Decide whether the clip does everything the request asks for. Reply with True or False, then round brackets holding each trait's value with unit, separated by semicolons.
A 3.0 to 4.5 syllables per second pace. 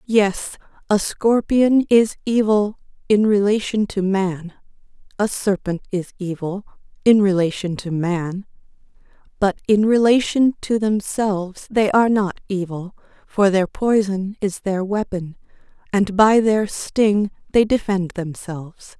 True (4.0 syllables/s)